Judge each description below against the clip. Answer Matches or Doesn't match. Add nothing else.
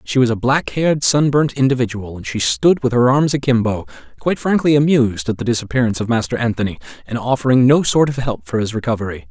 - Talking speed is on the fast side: Matches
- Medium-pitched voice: Doesn't match